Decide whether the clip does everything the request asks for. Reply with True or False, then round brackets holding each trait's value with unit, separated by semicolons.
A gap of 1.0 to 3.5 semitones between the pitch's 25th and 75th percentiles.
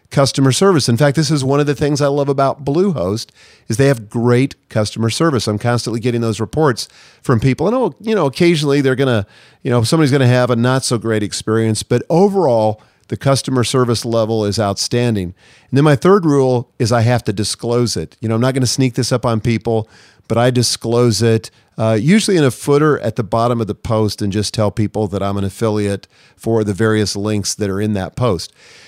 False (3.9 semitones)